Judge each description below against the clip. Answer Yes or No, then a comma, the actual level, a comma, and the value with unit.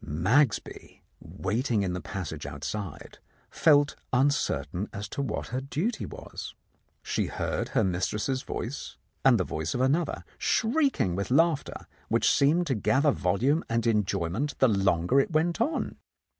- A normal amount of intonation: No, wide, 7.1 semitones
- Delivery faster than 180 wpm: No, average, 155 wpm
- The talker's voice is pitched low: Yes, low, 125 Hz